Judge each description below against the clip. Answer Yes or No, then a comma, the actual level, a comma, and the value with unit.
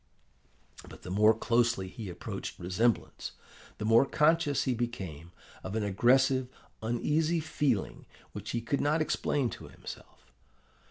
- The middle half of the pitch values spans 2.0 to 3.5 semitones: No, average, 5.2 semitones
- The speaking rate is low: Yes, slow, 130 wpm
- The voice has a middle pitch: No, low, 120 Hz